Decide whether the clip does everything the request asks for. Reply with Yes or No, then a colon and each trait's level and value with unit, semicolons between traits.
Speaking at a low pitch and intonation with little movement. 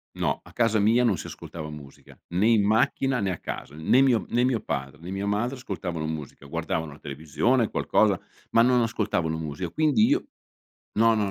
No: low, 100 Hz; wide, 6.8 semitones